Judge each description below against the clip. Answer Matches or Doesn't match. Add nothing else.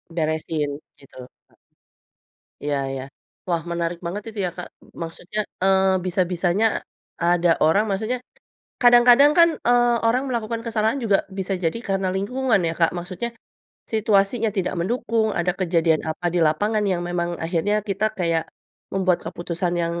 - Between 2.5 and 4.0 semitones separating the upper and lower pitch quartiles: Doesn't match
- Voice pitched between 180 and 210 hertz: Matches